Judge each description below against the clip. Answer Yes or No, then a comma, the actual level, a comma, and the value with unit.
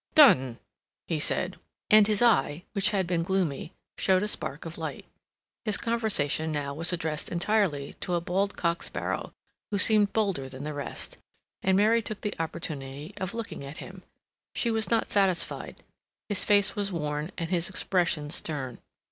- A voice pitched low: No, medium, 180 Hz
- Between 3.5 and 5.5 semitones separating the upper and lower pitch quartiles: Yes, average, 5.2 semitones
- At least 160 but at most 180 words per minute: Yes, average, 165 wpm